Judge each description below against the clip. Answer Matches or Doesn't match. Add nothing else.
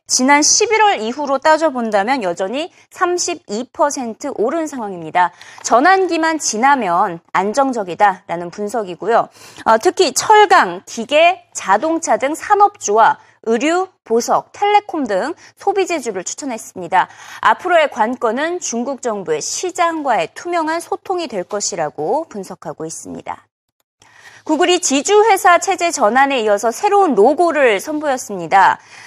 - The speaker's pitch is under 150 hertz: Doesn't match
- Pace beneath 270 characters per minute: Doesn't match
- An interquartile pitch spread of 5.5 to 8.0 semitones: Doesn't match